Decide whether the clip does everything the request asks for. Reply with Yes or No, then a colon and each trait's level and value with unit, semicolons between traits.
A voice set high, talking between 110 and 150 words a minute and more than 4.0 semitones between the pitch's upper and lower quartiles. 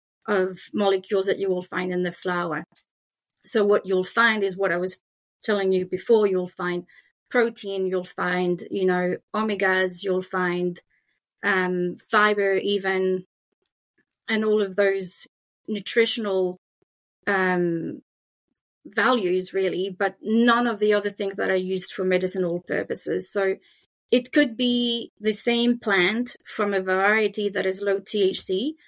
No: high, 195 Hz; average, 140 wpm; narrow, 2.6 semitones